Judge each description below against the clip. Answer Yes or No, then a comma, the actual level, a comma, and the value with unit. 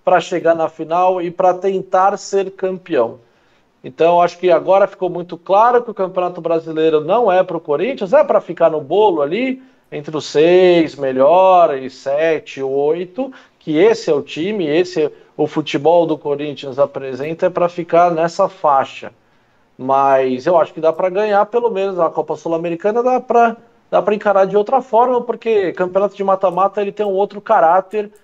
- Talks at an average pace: Yes, average, 175 wpm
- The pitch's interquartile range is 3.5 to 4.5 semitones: Yes, average, 4.1 semitones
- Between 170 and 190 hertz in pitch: Yes, medium, 185 Hz